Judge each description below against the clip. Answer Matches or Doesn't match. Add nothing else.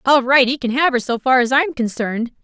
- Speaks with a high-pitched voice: Matches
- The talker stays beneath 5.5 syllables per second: Doesn't match